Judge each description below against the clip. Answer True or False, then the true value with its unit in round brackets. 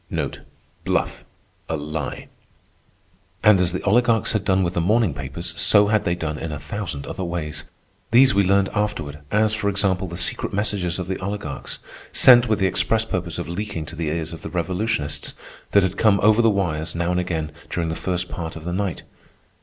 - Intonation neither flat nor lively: True (3.9 semitones)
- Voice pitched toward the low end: True (90 Hz)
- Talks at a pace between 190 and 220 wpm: True (195 wpm)